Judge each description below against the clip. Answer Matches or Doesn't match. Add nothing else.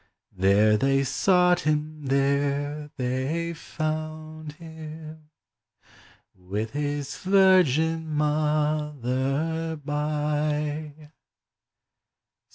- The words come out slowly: Matches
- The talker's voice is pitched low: Doesn't match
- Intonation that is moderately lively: Doesn't match